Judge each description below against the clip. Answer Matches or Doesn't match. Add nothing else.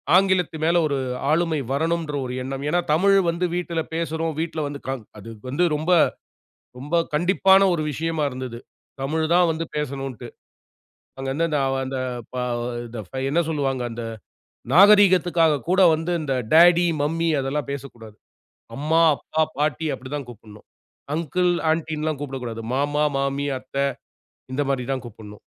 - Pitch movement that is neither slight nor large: Matches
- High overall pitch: Doesn't match